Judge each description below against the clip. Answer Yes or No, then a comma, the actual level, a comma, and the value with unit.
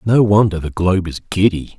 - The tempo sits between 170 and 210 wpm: Yes, average, 200 wpm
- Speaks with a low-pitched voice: Yes, very low, 95 Hz